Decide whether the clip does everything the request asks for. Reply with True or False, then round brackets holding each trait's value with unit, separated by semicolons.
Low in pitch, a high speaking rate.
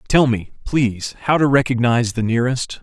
False (125 Hz; 170 wpm)